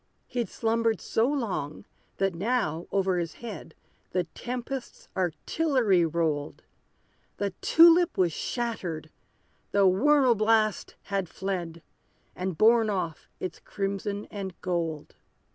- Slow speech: Yes, slow, 110 wpm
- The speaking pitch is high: Yes, high, 195 Hz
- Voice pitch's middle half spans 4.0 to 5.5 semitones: Yes, average, 5.0 semitones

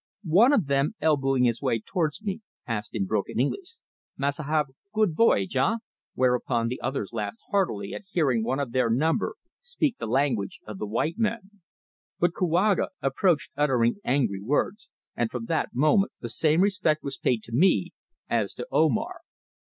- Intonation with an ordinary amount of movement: No, wide, 7.6 semitones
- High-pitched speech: No, medium, 140 Hz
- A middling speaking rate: Yes, average, 170 wpm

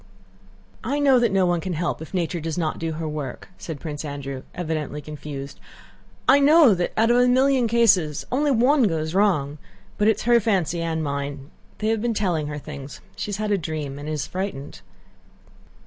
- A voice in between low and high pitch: Yes, medium, 170 Hz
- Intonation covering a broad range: Yes, wide, 6.7 semitones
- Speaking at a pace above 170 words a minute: Yes, average, 195 wpm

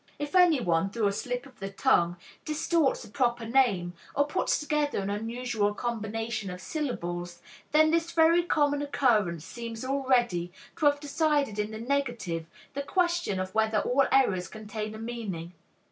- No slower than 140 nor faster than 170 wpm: Yes, average, 160 wpm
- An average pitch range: No, wide, 6.0 semitones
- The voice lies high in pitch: Yes, high, 235 Hz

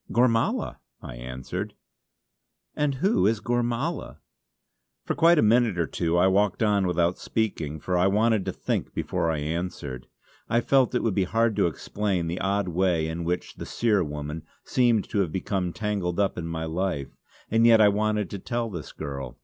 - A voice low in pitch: Yes, very low, 95 Hz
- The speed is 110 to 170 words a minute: No, average, 185 wpm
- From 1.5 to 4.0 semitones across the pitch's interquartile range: No, average, 5.2 semitones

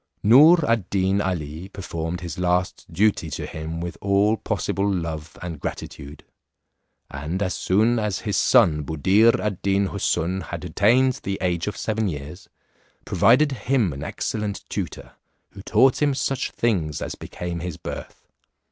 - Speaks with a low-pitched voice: Yes, very low, 95 Hz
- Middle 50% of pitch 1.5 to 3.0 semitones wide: No, average, 4.3 semitones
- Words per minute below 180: Yes, average, 150 wpm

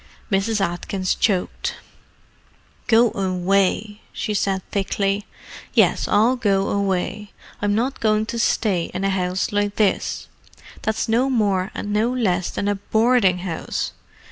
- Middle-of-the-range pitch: No, high, 205 Hz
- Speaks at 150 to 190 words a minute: No, slow, 135 wpm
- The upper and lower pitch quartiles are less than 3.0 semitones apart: Yes, narrow, 2.4 semitones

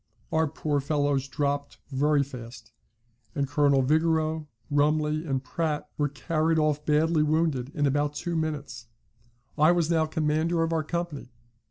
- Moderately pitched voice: Yes, medium, 150 Hz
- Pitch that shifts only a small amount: Yes, narrow, 2.0 semitones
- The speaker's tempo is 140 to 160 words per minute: Yes, average, 145 wpm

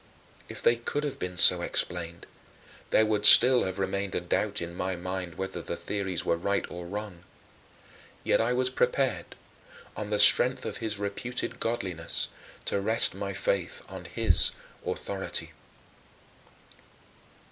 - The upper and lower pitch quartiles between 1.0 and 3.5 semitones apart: No, average, 4.6 semitones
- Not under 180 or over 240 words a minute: No, average, 145 wpm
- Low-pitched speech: Yes, low, 100 Hz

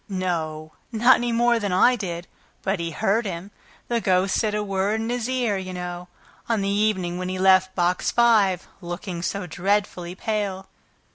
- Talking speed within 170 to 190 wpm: Yes, average, 180 wpm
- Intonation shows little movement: No, average, 3.3 semitones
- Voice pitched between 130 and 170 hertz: No, high, 195 Hz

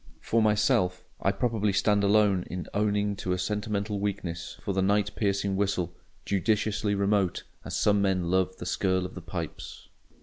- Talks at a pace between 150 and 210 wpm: Yes, average, 160 wpm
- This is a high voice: No, low, 100 Hz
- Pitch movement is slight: Yes, narrow, 1.9 semitones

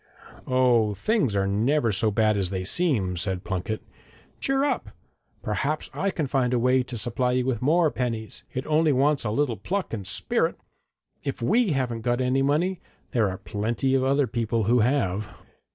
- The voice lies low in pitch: Yes, low, 125 Hz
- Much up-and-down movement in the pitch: No, average, 4.8 semitones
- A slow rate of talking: No, average, 180 wpm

